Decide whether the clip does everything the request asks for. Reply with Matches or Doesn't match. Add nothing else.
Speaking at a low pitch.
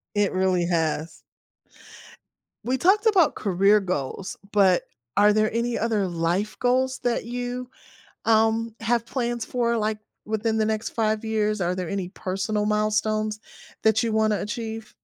Doesn't match